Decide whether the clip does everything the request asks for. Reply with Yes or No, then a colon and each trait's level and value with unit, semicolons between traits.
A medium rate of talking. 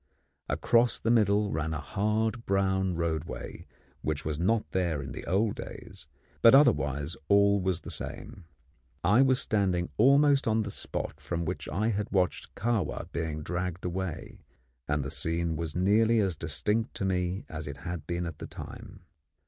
Yes: average, 165 wpm